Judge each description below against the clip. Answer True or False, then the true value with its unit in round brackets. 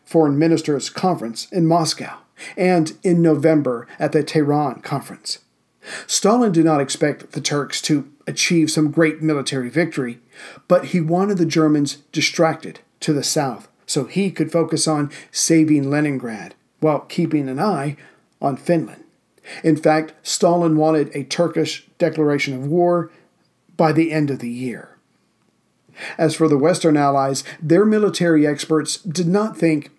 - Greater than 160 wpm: False (145 wpm)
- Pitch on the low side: False (155 Hz)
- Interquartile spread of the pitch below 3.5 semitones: True (2.6 semitones)